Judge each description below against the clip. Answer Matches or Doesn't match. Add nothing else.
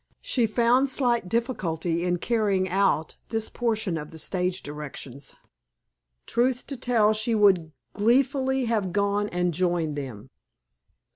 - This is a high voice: Matches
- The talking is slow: Matches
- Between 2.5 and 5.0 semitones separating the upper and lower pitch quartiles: Doesn't match